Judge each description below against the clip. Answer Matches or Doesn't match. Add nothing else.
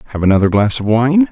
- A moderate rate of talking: Doesn't match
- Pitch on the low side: Matches